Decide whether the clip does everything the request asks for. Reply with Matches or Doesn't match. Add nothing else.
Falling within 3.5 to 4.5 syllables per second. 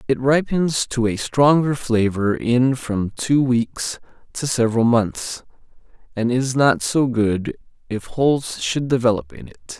Matches